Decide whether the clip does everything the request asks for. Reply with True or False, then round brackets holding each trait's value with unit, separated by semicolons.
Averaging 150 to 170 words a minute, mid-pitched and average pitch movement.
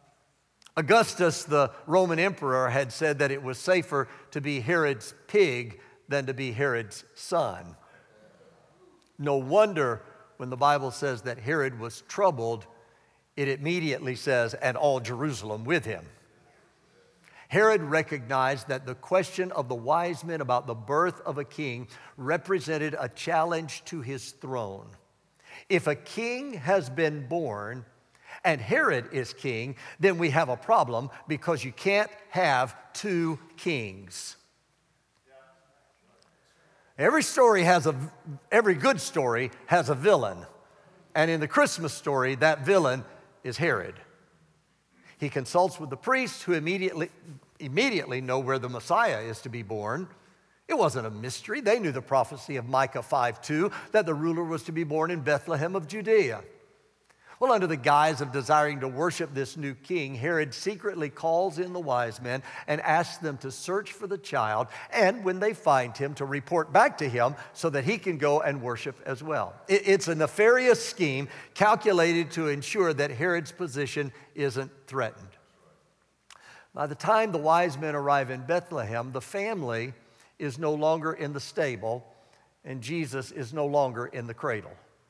True (155 wpm; 150 Hz; 4.7 semitones)